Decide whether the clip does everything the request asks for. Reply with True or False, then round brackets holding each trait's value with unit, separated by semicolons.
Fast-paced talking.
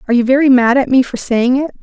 True (295 wpm)